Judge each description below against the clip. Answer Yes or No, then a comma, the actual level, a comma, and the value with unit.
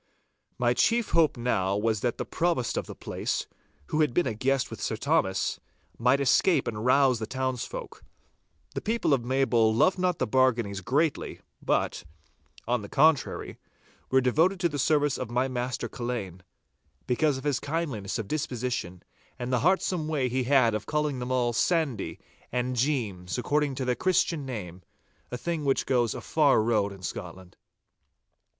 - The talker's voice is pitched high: No, low, 125 Hz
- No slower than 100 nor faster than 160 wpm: No, average, 170 wpm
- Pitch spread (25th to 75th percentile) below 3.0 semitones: No, average, 4.4 semitones